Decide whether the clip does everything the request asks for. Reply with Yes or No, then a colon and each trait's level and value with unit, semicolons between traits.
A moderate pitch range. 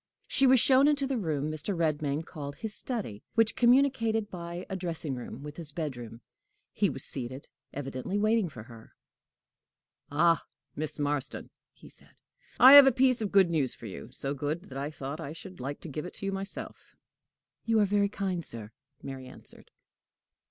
No: wide, 6.9 semitones